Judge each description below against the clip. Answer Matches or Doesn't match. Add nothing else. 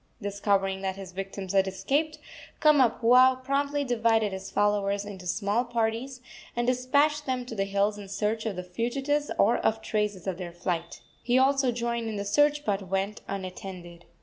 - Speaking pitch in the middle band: Doesn't match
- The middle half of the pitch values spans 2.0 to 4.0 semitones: Doesn't match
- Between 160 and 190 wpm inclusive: Matches